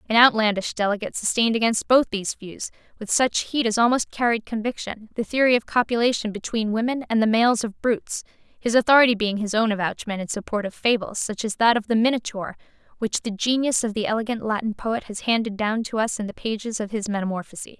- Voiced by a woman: Yes, female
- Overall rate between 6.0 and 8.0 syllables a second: Yes, 6.1 syllables/s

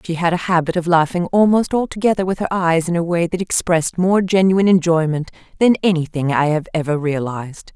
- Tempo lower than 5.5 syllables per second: No, 5.9 syllables/s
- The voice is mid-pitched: Yes, medium, 175 Hz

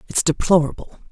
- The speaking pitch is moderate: Yes, medium, 165 Hz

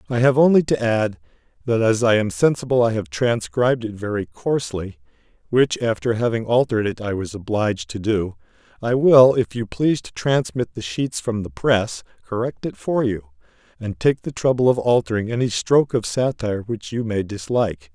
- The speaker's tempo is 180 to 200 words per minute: Yes, average, 185 wpm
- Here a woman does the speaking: No, male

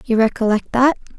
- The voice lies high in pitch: Yes, high, 235 Hz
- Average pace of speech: Yes, average, 150 wpm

